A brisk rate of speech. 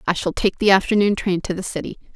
Yes: fast, 250 wpm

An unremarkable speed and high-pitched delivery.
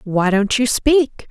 Yes: average, 185 wpm; high, 230 Hz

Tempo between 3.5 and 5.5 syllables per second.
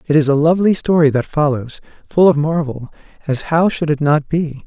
Yes: 5.4 syllables/s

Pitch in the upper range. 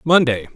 No: low, 135 Hz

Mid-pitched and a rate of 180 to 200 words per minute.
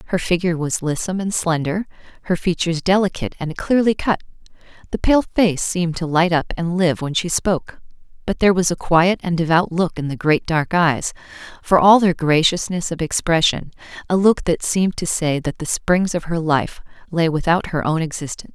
Yes: medium, 170 Hz; average, 190 wpm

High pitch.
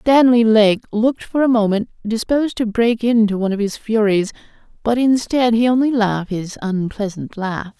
Yes: high, 220 Hz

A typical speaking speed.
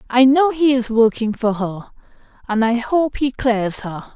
Yes: average, 190 wpm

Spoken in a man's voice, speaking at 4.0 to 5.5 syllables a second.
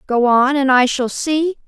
No: female; 4.1 syllables/s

